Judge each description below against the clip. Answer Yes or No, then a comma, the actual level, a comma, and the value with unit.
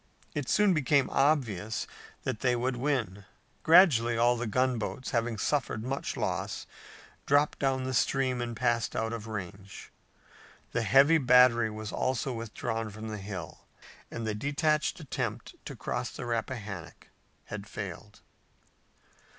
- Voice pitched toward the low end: Yes, low, 120 Hz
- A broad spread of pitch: No, average, 3.6 semitones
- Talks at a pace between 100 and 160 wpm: Yes, average, 140 wpm